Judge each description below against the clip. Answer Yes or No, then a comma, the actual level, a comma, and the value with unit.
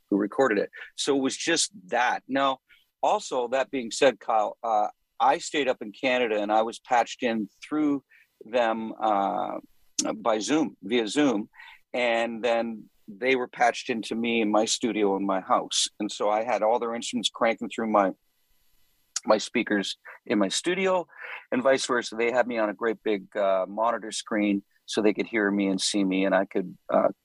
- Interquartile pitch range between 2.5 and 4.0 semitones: Yes, average, 3.2 semitones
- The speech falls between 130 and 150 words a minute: No, average, 185 wpm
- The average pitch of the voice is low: Yes, low, 115 Hz